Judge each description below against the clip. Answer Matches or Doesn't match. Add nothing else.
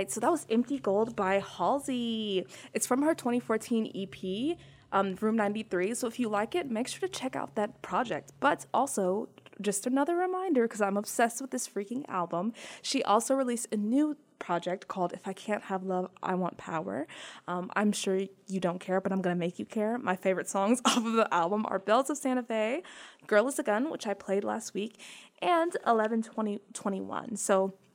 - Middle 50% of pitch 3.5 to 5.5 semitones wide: Matches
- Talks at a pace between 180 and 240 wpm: Matches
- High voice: Matches